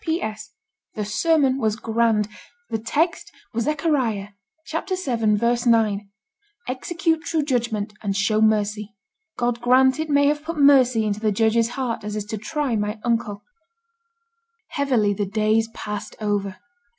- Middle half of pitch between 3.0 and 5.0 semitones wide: Yes, average, 4.5 semitones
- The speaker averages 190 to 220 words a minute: No, average, 140 wpm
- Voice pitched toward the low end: No, high, 230 Hz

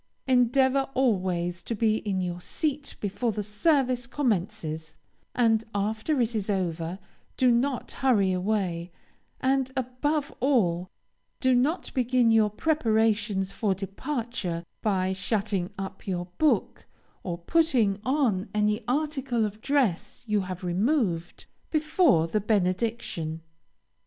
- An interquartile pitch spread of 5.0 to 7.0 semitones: Yes, wide, 5.5 semitones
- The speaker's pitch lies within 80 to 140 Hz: No, high, 215 Hz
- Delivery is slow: Yes, slow, 120 wpm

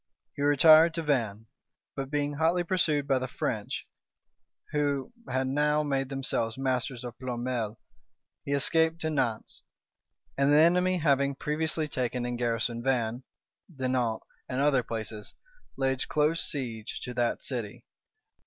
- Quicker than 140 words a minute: No, slow, 135 wpm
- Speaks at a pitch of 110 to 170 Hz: Yes, low, 135 Hz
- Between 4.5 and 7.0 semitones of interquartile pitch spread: No, average, 3.5 semitones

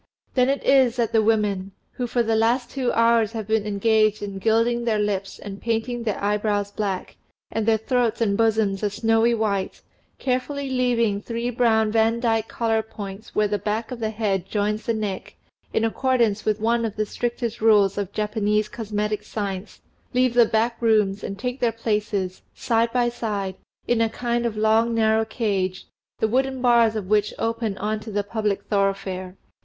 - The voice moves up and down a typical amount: No, narrow, 2.1 semitones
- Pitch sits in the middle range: No, high, 220 Hz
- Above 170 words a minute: Yes, average, 180 wpm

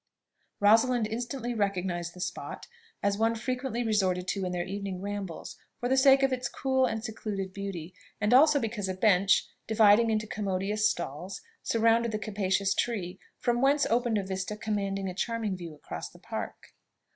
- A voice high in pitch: Yes, high, 210 Hz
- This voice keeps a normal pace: Yes, average, 170 wpm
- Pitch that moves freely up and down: No, average, 3.6 semitones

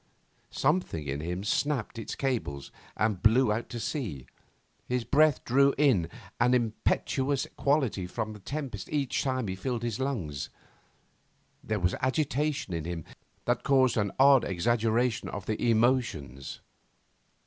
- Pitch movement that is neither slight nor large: No, wide, 5.8 semitones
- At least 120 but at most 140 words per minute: Yes, slow, 135 wpm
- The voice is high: No, low, 120 Hz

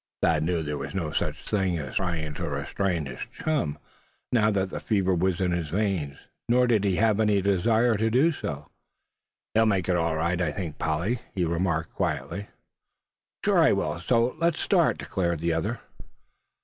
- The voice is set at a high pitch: No, very low, 90 Hz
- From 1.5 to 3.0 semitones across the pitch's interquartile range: No, average, 4.6 semitones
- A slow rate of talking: No, average, 180 wpm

